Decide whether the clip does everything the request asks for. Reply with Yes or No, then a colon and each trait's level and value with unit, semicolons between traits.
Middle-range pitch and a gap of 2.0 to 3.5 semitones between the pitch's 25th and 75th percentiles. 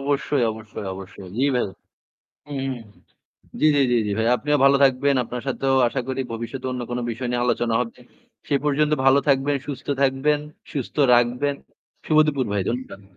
No: low, 130 Hz; average, 2.8 semitones